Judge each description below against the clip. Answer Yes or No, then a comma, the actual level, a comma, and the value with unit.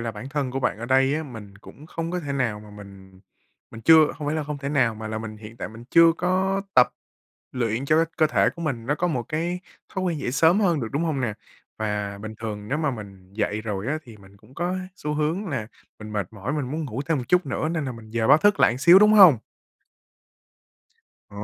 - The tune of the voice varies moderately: No, wide, 6.4 semitones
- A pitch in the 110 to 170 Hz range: Yes, low, 135 Hz